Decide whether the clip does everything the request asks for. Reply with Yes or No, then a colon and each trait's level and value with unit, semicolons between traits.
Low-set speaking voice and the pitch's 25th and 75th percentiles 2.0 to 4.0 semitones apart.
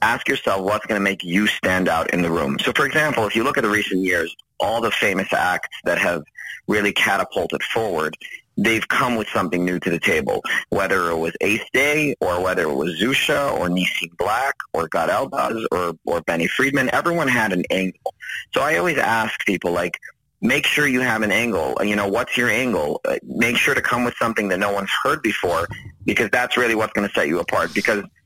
Yes: very low, 95 Hz; average, 3.3 semitones